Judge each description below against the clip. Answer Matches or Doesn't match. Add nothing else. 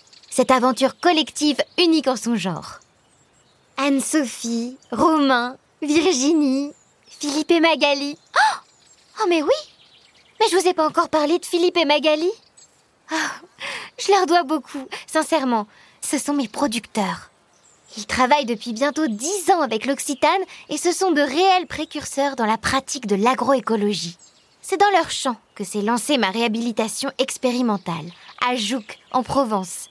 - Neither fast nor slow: Doesn't match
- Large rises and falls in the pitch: Doesn't match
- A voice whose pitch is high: Matches